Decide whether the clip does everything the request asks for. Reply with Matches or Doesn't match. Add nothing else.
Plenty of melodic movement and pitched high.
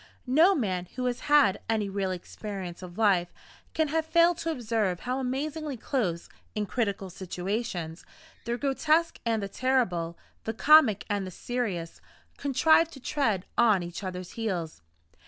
Matches